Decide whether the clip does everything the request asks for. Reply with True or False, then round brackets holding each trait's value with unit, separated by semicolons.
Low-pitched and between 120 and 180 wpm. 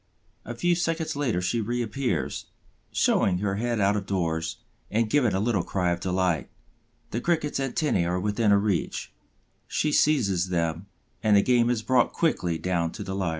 True (105 Hz; 175 wpm)